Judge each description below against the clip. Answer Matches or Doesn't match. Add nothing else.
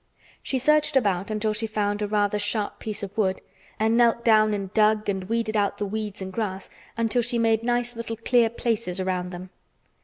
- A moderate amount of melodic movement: Doesn't match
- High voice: Matches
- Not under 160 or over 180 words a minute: Doesn't match